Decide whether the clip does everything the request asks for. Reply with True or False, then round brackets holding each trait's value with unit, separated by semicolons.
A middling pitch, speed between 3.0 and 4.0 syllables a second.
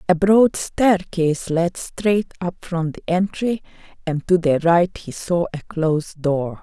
True (175 Hz; 3.8 syllables/s)